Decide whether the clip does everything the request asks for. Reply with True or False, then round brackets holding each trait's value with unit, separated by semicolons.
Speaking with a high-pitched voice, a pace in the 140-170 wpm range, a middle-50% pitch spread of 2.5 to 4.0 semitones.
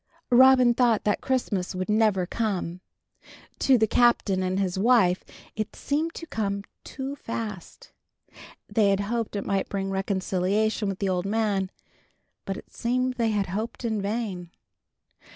True (210 Hz; 150 wpm; 3.5 semitones)